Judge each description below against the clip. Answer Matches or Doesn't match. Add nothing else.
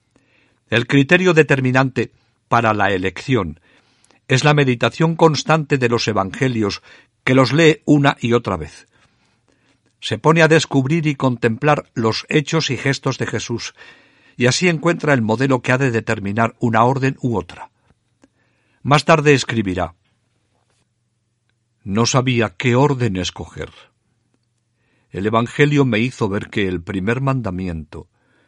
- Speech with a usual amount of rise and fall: Matches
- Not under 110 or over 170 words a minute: Matches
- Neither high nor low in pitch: Doesn't match